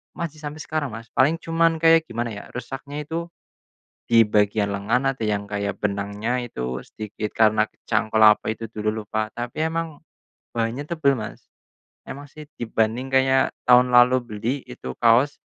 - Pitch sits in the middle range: No, low, 120 Hz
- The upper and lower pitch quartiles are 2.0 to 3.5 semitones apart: No, average, 5.0 semitones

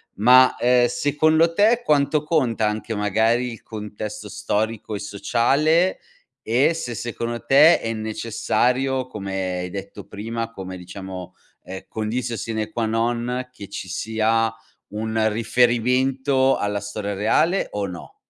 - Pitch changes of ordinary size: Yes, average, 3.5 semitones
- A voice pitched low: Yes, low, 115 Hz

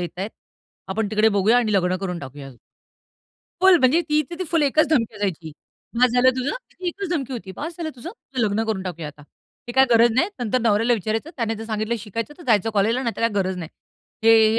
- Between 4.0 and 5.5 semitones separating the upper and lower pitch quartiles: Yes, average, 4.6 semitones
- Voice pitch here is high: Yes, high, 225 Hz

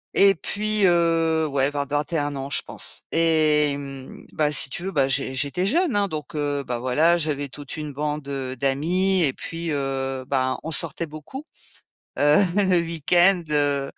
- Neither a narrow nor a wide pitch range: Yes, average, 3.3 semitones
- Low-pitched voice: No, medium, 150 Hz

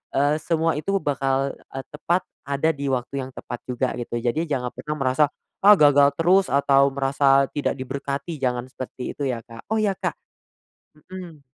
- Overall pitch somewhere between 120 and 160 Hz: Yes, medium, 140 Hz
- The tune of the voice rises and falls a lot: No, average, 2.7 semitones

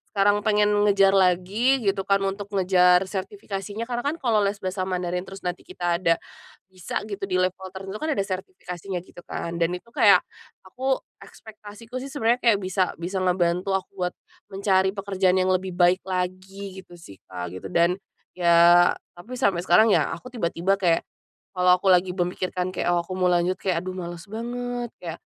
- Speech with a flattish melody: Yes, narrow, 2.2 semitones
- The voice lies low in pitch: No, high, 190 Hz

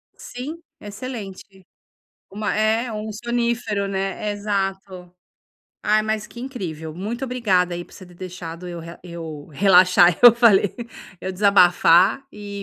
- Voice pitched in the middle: No, high, 200 Hz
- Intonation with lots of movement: No, average, 3.3 semitones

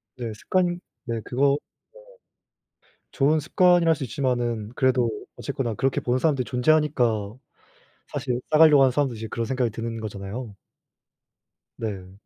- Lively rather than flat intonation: No, average, 4.0 semitones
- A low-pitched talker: Yes, low, 125 Hz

